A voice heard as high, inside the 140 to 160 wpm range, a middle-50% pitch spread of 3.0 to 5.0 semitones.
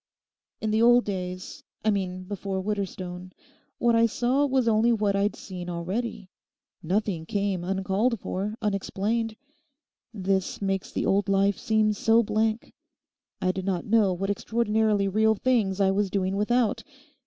No: high, 205 Hz; average, 145 wpm; narrow, 2.6 semitones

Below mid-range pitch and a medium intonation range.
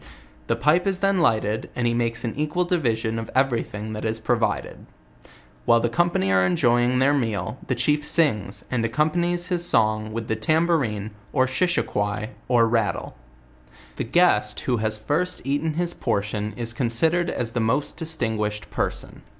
No: low, 120 Hz; wide, 5.9 semitones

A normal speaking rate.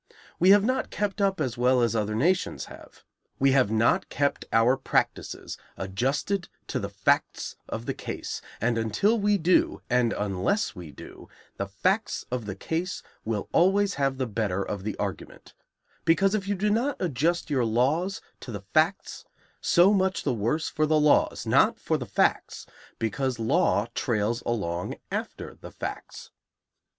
Yes: average, 165 wpm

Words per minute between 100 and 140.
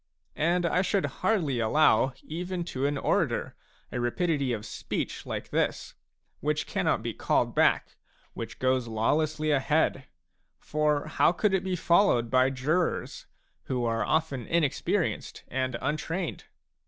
Yes: slow, 135 wpm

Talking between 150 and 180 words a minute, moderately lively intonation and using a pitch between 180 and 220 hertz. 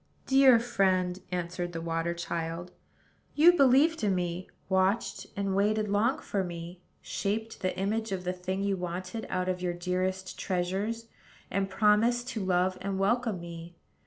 Yes: average, 155 wpm; average, 3.2 semitones; high, 190 Hz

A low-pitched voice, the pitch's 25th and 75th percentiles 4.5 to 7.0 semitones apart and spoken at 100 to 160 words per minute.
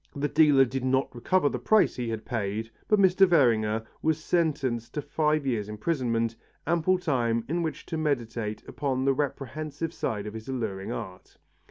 No: low, 130 Hz; wide, 5.4 semitones; average, 170 wpm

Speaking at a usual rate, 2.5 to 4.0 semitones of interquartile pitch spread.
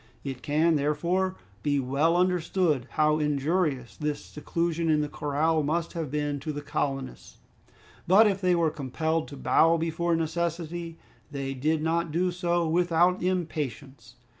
Yes: average, 145 wpm; average, 2.8 semitones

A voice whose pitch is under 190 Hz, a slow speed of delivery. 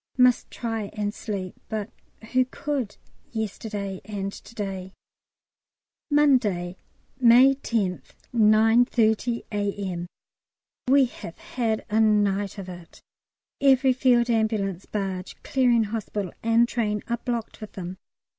No: high, 215 Hz; slow, 115 wpm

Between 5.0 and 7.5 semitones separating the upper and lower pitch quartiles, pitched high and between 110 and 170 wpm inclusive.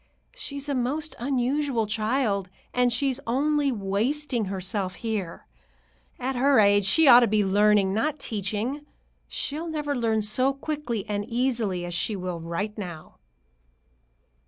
Yes: average, 5.3 semitones; high, 230 Hz; slow, 135 wpm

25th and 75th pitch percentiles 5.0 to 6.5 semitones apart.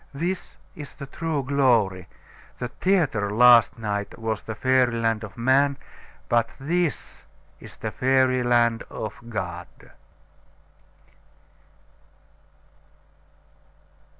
No: average, 3.8 semitones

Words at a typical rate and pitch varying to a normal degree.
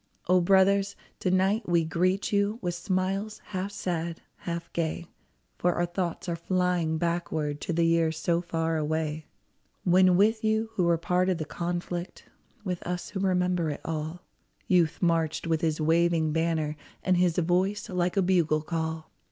No: average, 170 wpm; narrow, 2.2 semitones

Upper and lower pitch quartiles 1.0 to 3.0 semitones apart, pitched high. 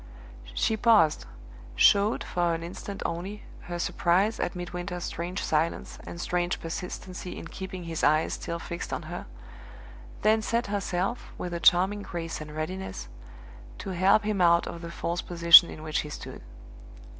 No: narrow, 2.5 semitones; medium, 175 Hz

